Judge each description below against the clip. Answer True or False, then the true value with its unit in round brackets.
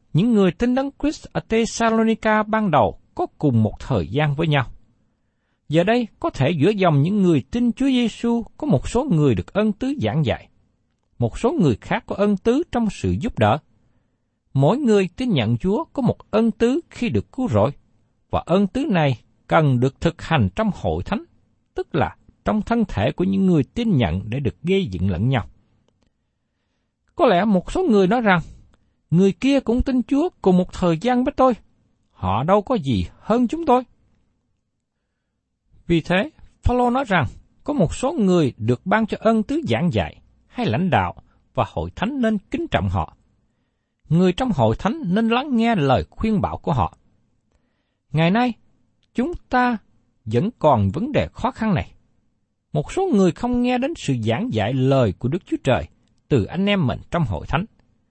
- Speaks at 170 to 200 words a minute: True (190 wpm)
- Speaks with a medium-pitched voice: True (175 Hz)